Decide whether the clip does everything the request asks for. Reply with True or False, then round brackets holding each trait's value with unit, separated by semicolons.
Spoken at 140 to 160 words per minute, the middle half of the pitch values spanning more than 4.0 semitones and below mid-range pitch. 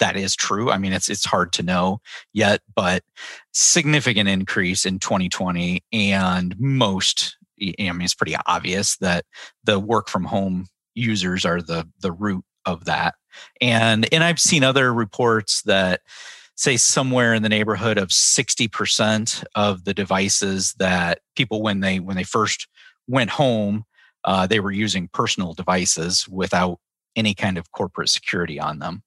False (155 wpm; 3.1 semitones; 100 Hz)